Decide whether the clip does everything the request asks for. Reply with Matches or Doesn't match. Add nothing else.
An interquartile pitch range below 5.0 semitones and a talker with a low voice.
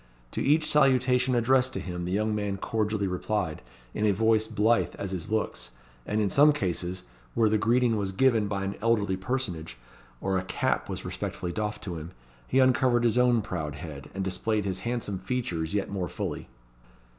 Matches